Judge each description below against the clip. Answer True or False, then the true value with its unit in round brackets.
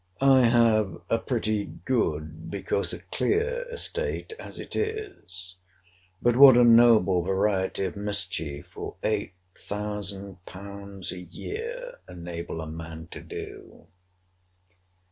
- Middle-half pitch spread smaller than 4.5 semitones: False (5.0 semitones)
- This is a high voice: False (100 Hz)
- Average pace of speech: False (110 wpm)